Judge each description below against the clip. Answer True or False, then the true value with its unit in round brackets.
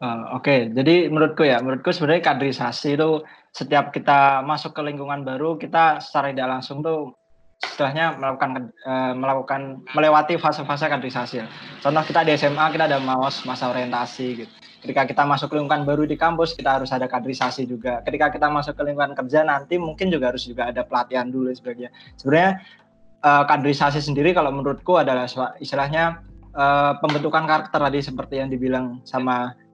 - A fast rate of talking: True (165 wpm)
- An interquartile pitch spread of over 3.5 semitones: False (2.9 semitones)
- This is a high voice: False (140 Hz)